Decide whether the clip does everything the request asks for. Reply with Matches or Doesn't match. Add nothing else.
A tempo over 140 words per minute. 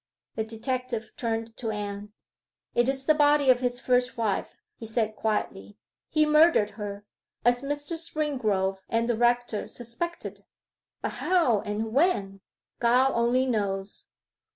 Doesn't match